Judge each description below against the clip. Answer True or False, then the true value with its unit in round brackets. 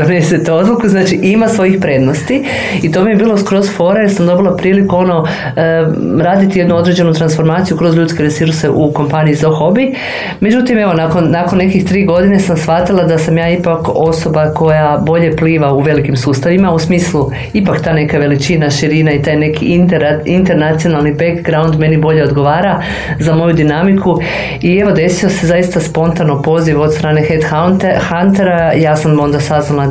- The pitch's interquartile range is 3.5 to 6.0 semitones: False (2.8 semitones)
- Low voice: False (165 Hz)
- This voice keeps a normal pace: False (165 wpm)